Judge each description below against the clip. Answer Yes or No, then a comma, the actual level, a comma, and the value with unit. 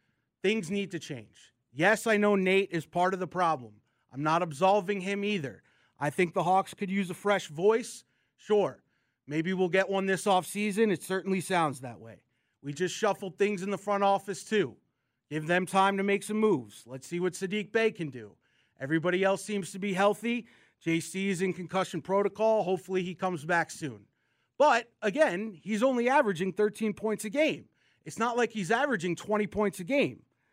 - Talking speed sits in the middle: Yes, average, 190 wpm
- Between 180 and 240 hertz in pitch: Yes, high, 190 Hz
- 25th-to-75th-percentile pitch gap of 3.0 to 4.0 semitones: Yes, average, 3.6 semitones